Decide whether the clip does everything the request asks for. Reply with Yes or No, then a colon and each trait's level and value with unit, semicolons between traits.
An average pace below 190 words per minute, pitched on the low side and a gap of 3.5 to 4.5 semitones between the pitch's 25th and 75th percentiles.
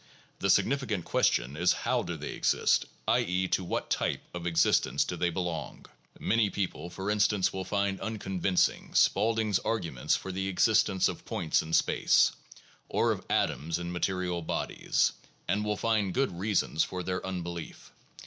No: average, 160 wpm; very low, 95 Hz; average, 3.1 semitones